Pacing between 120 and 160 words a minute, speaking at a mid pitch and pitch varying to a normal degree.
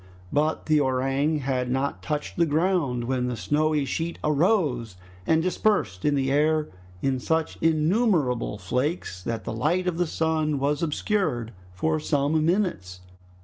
Yes: average, 145 wpm; medium, 150 Hz; average, 3.9 semitones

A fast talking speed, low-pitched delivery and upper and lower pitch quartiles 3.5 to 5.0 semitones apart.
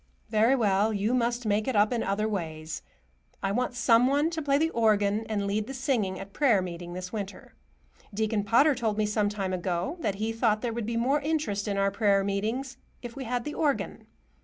No: fast, 210 wpm; high, 215 Hz; average, 3.8 semitones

